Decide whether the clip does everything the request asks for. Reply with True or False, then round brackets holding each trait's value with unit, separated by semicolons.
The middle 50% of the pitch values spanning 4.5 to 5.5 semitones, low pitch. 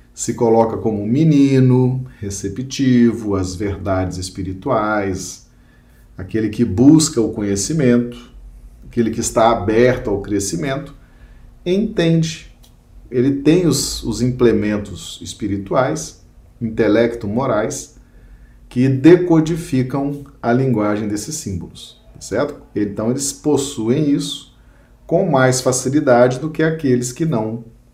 True (4.9 semitones; 120 Hz)